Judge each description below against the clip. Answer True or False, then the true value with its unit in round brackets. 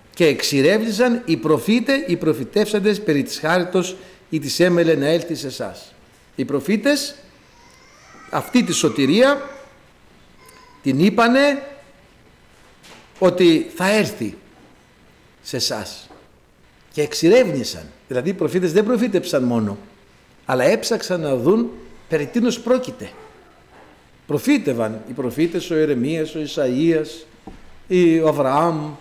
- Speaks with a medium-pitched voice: True (170 Hz)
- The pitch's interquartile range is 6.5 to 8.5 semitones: True (7.0 semitones)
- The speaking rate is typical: False (110 wpm)